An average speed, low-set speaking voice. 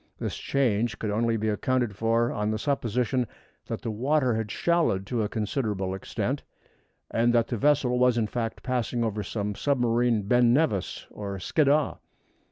Yes: average, 165 wpm; low, 115 Hz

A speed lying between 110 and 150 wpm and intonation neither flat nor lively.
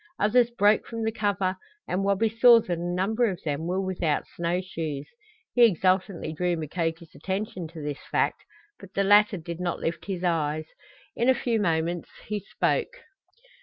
No: average, 170 wpm; average, 3.8 semitones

